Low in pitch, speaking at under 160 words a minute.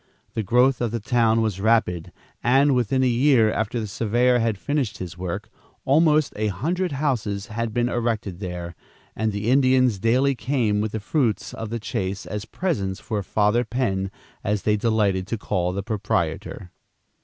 No: low, 110 Hz; average, 170 wpm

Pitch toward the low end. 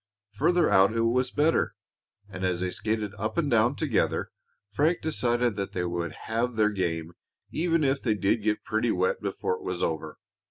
Yes: low, 115 Hz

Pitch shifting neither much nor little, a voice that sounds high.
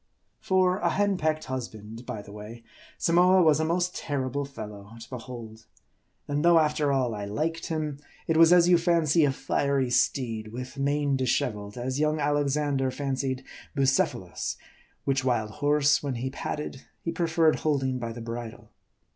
No: average, 4.4 semitones; medium, 140 Hz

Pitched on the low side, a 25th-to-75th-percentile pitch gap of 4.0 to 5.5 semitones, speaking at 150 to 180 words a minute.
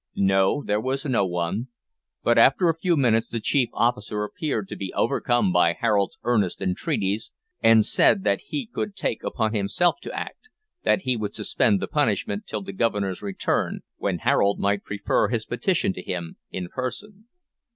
Yes: low, 110 Hz; average, 4.6 semitones; average, 170 wpm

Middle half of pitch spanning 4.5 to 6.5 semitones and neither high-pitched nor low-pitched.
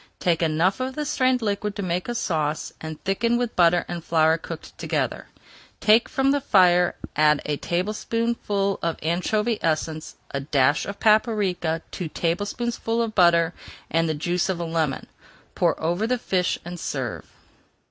Yes: average, 5.0 semitones; medium, 180 Hz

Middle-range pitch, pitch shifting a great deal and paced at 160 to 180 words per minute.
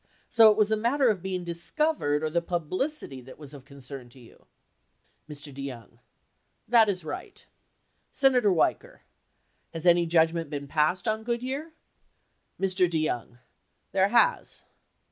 No: medium, 175 Hz; wide, 6.9 semitones; average, 145 wpm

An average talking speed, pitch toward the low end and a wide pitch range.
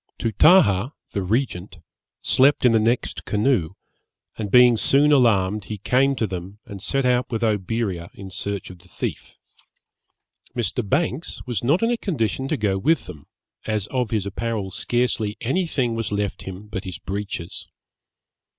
No: average, 160 wpm; low, 110 Hz; average, 4.5 semitones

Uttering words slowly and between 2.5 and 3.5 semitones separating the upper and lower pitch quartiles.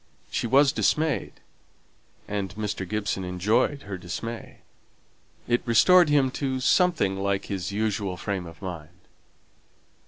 No: slow, 120 wpm; wide, 5.4 semitones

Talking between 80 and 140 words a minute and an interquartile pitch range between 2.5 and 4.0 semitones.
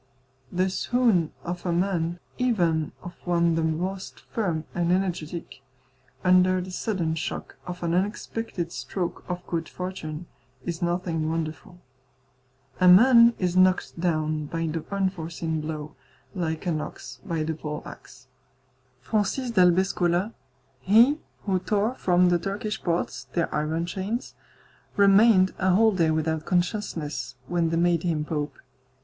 Yes: slow, 135 wpm; average, 2.9 semitones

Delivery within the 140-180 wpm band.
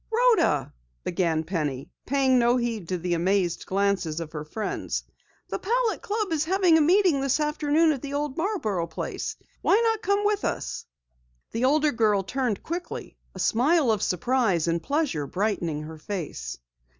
Yes: average, 160 wpm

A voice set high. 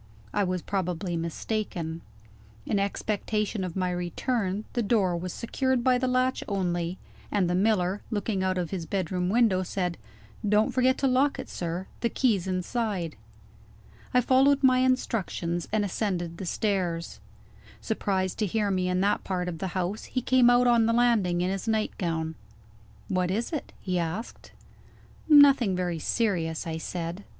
Yes: high, 195 Hz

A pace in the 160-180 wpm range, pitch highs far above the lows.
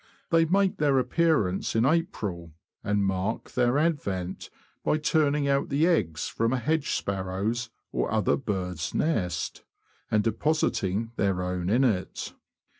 No: slow, 135 wpm; wide, 8.0 semitones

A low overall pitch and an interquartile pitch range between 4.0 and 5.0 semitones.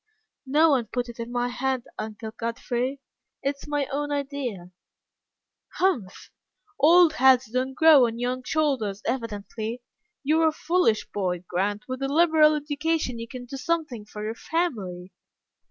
No: very high, 255 Hz; average, 4.6 semitones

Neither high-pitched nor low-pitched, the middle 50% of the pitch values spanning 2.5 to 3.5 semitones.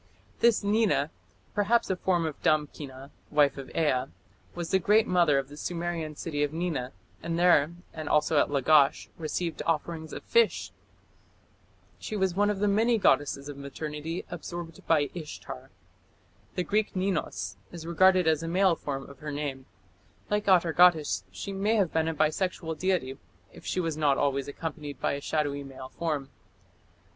No: medium, 160 Hz; average, 3.9 semitones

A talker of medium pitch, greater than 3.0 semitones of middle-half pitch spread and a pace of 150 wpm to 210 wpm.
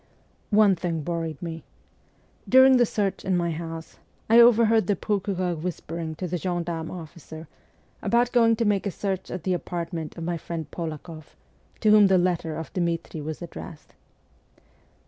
Yes: medium, 175 Hz; average, 3.6 semitones; average, 160 wpm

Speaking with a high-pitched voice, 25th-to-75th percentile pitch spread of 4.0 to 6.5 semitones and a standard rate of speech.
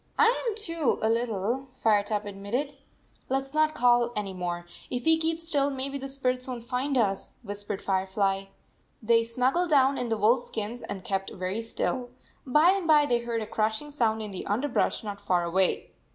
Yes: high, 235 Hz; average, 5.1 semitones; average, 195 wpm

